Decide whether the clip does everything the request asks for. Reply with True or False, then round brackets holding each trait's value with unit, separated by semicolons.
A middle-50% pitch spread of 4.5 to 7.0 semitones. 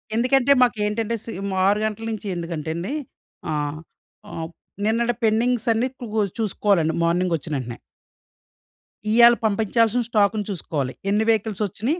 True (5.0 semitones)